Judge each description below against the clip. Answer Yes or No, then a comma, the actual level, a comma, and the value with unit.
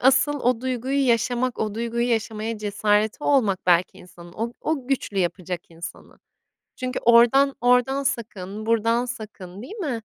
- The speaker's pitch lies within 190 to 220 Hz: No, high, 230 Hz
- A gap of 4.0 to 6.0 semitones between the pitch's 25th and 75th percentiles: No, average, 3.6 semitones